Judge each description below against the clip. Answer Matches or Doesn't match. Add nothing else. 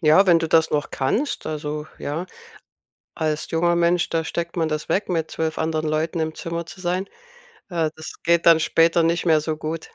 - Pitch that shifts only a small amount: Matches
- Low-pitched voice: Doesn't match